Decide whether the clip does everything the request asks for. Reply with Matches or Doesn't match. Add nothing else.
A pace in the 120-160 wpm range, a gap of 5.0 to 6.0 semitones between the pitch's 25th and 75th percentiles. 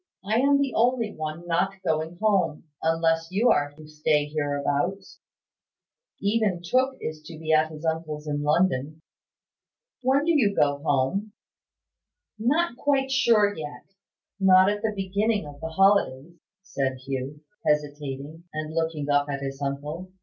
Matches